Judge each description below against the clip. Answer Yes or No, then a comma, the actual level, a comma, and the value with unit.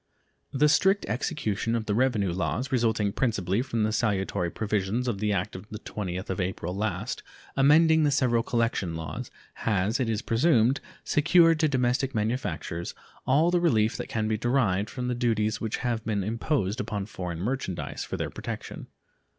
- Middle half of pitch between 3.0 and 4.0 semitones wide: No, average, 4.4 semitones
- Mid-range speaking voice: No, low, 115 Hz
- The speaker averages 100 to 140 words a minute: No, average, 170 wpm